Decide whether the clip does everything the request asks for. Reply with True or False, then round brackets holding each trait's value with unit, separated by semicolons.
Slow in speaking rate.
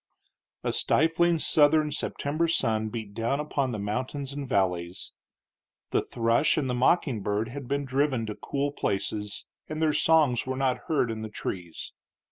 False (165 wpm)